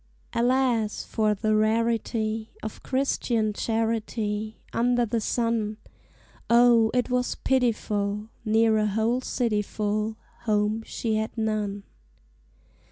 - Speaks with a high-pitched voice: Yes, high, 220 Hz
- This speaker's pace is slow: Yes, slow, 105 wpm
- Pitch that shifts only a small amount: Yes, narrow, 1.6 semitones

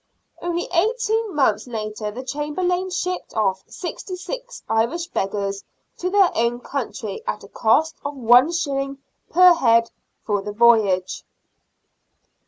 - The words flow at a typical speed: No, slow, 130 wpm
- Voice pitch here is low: No, very high, 275 Hz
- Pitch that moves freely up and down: Yes, wide, 8.4 semitones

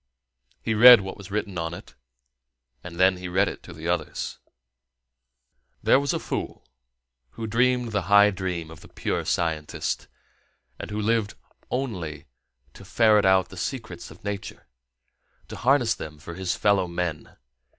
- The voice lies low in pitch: Yes, very low, 95 Hz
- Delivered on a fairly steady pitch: No, average, 4.1 semitones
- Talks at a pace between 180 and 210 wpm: No, average, 155 wpm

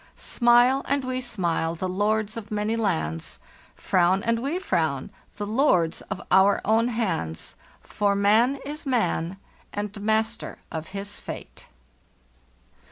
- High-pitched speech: Yes, high, 210 Hz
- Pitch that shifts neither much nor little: Yes, average, 4.1 semitones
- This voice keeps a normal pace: No, slow, 130 wpm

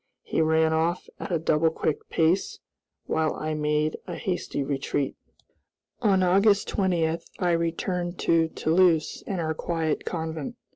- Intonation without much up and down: Yes, narrow, 2.1 semitones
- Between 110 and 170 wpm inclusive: Yes, average, 140 wpm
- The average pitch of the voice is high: No, medium, 165 Hz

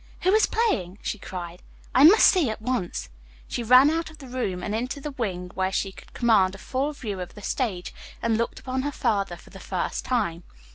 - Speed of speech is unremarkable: No, fast, 220 wpm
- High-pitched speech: Yes, high, 230 Hz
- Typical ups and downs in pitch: No, wide, 5.9 semitones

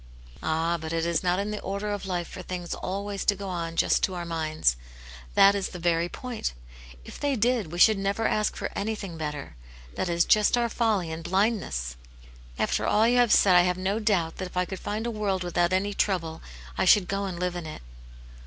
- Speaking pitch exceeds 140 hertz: Yes, medium, 185 Hz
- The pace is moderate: No, fast, 225 wpm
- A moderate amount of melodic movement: Yes, average, 3.3 semitones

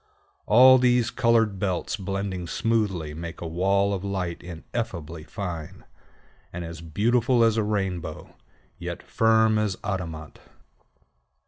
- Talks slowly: Yes, slow, 120 wpm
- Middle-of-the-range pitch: No, low, 100 Hz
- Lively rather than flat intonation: No, average, 4.6 semitones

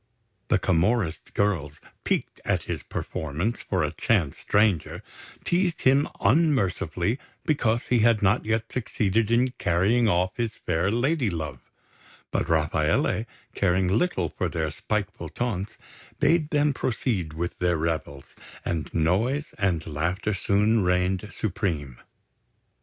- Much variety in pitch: Yes, wide, 5.7 semitones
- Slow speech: Yes, slow, 125 wpm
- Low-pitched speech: Yes, low, 100 Hz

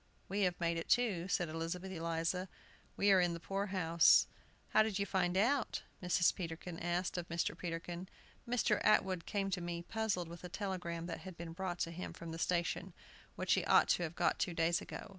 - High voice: No, medium, 175 Hz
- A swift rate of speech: Yes, fast, 210 wpm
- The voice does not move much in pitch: Yes, narrow, 2.3 semitones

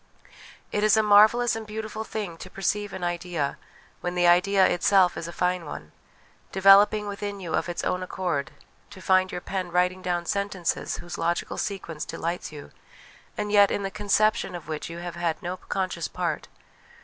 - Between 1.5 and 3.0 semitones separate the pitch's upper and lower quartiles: Yes, average, 2.7 semitones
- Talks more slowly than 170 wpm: No, average, 180 wpm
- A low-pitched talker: No, medium, 185 Hz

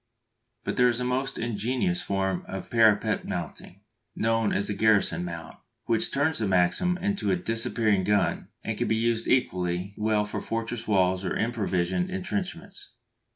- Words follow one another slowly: No, average, 155 wpm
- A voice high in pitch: No, low, 110 Hz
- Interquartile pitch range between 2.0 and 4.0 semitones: No, average, 4.4 semitones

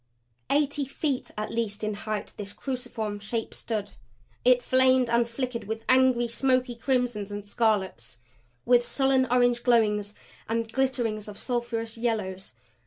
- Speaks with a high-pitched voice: Yes, high, 235 Hz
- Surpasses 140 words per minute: No, slow, 135 wpm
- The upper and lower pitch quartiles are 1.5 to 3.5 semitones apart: Yes, average, 3.0 semitones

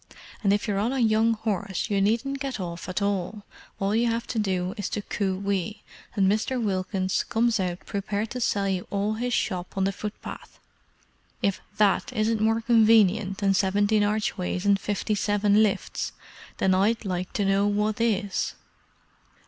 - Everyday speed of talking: Yes, average, 170 wpm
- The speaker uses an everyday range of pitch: No, narrow, 2.1 semitones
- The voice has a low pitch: No, high, 205 Hz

